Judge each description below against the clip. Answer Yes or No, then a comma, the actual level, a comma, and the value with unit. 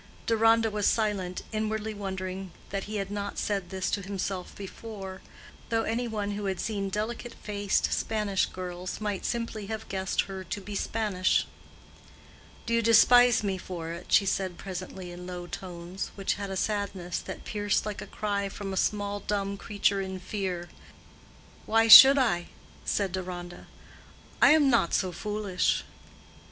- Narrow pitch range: Yes, narrow, 2.3 semitones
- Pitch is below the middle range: No, high, 200 Hz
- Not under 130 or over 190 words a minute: Yes, average, 160 wpm